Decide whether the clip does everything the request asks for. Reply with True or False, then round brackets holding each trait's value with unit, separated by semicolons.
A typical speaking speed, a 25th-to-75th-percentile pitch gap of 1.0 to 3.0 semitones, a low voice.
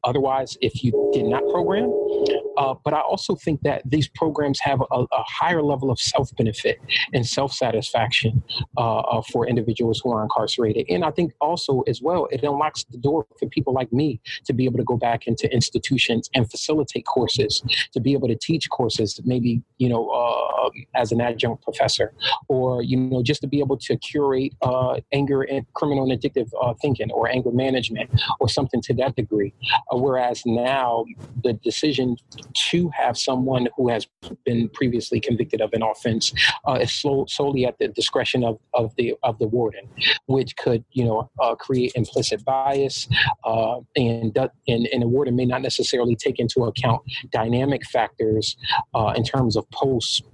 True (175 wpm; 2.7 semitones; 130 Hz)